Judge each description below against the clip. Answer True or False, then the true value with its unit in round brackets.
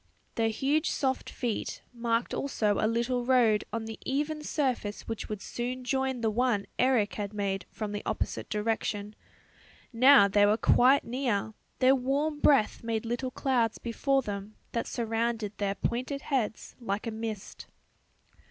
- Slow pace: False (150 wpm)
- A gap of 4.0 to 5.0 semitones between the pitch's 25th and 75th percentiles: False (3.5 semitones)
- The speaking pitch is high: True (230 Hz)